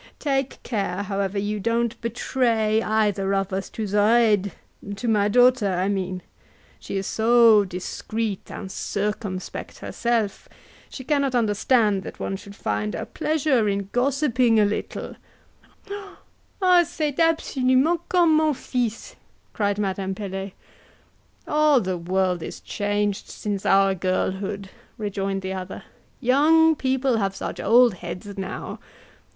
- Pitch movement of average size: Yes, average, 4.4 semitones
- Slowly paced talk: Yes, slow, 130 wpm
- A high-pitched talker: Yes, high, 210 Hz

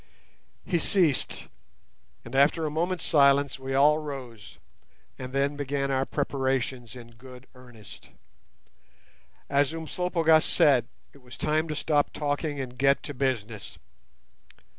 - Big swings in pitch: No, average, 2.9 semitones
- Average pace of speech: No, slow, 125 wpm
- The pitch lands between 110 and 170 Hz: Yes, medium, 140 Hz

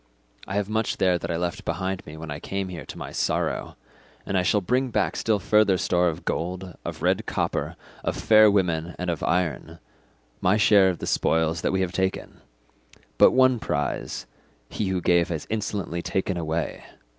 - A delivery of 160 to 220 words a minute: Yes, average, 190 wpm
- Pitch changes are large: No, average, 3.0 semitones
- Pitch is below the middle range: Yes, very low, 90 Hz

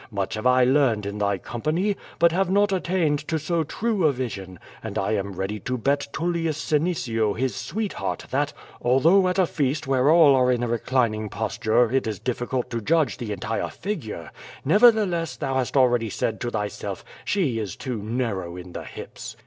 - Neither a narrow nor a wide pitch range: No, wide, 6.8 semitones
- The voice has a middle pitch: No, low, 130 Hz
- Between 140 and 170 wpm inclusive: No, average, 190 wpm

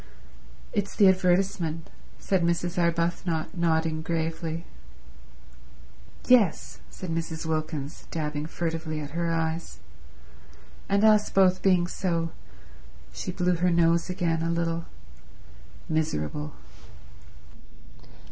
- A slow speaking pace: Yes, slow, 90 wpm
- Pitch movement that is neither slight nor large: No, narrow, 1.9 semitones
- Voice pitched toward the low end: No, medium, 165 Hz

